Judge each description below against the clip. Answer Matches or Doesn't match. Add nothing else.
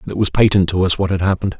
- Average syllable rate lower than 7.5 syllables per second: Doesn't match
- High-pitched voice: Doesn't match